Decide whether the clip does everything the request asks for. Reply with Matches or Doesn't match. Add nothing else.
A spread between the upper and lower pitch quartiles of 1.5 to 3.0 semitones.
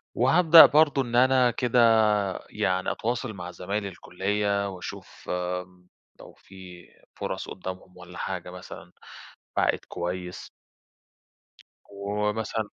Doesn't match